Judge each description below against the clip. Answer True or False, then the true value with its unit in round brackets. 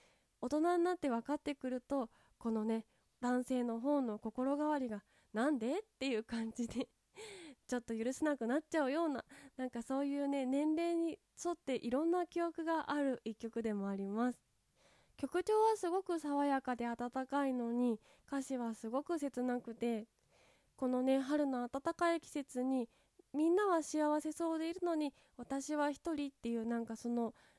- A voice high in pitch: True (275 Hz)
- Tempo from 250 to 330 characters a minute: True (315 characters per minute)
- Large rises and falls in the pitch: False (4.2 semitones)